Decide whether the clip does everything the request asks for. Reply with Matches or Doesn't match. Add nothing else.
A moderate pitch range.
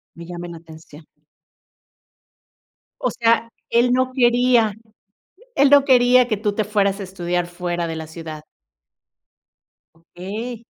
Doesn't match